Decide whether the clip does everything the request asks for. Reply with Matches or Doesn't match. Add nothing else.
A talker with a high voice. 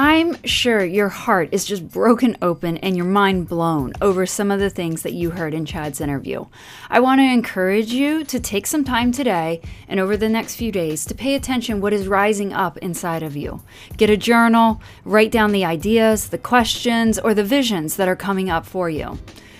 Matches